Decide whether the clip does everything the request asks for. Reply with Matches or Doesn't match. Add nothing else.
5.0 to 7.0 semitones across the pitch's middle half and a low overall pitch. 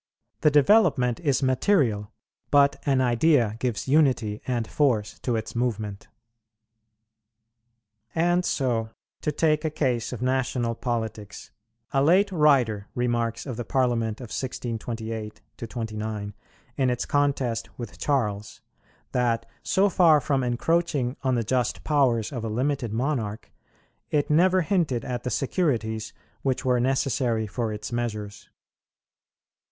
Doesn't match